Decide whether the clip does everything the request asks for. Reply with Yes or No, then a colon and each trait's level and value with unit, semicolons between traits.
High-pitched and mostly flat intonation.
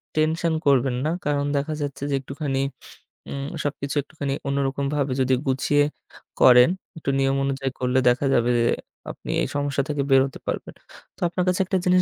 No: medium, 140 Hz; narrow, 1.8 semitones